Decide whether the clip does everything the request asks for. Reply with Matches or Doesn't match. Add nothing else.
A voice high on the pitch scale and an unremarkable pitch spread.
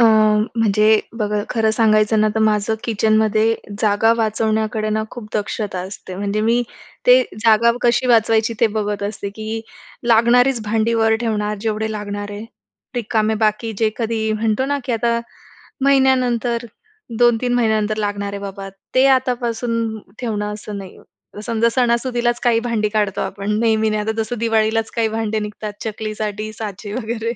Doesn't match